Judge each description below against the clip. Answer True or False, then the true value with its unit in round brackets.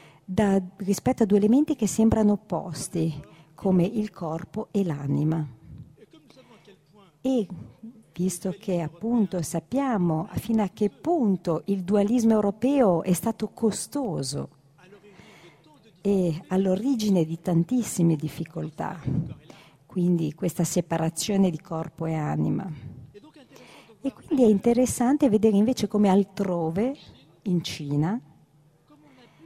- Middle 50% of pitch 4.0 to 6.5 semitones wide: True (5.0 semitones)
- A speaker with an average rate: False (100 wpm)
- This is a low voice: False (190 Hz)